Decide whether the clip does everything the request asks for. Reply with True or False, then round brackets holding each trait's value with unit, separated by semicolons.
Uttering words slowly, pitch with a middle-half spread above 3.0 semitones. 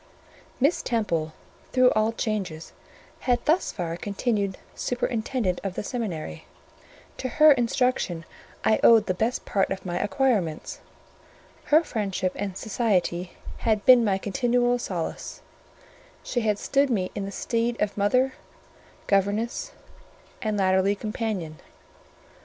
True (125 wpm; 4.3 semitones)